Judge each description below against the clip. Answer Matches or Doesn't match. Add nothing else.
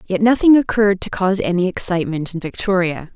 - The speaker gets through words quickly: Doesn't match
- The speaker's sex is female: Matches